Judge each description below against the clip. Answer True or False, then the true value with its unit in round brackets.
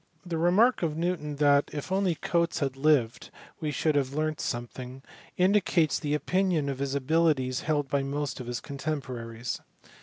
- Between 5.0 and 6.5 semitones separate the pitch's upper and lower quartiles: False (3.5 semitones)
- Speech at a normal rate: True (175 wpm)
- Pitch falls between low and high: True (150 Hz)